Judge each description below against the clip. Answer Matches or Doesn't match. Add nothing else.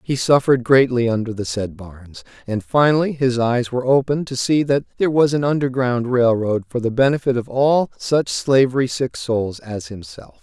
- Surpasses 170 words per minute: Matches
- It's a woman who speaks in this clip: Doesn't match